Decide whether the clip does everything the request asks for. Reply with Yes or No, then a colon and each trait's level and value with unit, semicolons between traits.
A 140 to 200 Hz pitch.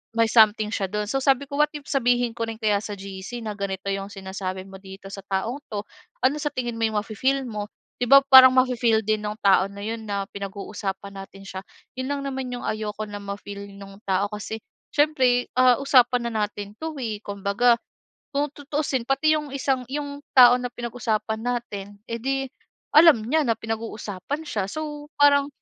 No: high, 225 Hz